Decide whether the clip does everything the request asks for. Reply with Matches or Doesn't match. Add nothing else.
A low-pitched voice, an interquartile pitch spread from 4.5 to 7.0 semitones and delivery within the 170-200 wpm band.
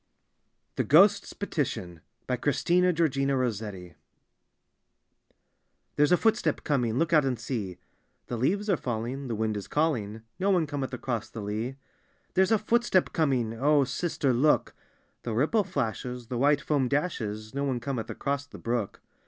Doesn't match